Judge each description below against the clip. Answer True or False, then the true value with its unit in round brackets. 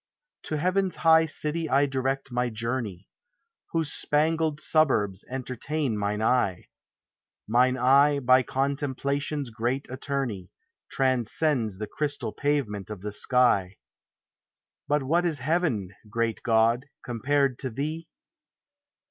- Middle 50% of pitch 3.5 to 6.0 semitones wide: True (4.4 semitones)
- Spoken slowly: True (115 wpm)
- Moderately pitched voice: False (130 Hz)